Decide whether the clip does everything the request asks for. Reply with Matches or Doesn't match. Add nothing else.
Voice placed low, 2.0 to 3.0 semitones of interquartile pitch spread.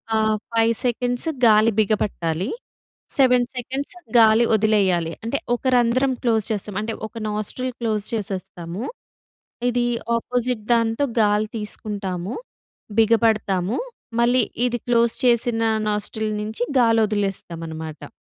Doesn't match